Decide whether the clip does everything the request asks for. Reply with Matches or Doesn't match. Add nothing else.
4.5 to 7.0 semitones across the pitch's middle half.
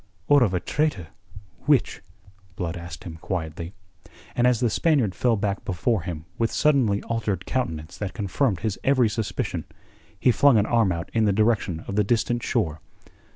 Matches